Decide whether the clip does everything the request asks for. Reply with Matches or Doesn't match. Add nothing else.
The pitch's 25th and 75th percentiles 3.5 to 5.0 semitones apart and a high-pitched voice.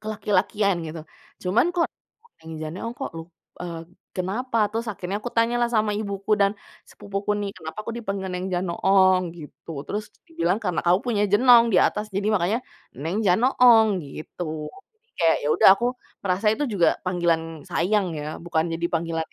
Matches